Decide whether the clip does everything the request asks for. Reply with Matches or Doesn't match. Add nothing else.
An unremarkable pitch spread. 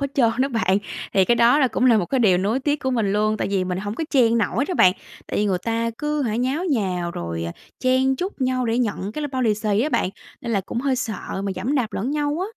Matches